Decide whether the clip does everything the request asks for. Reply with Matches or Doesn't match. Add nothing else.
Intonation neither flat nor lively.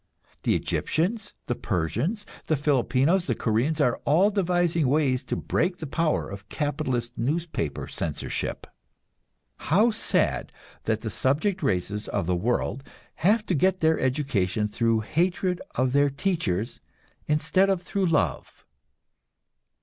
Doesn't match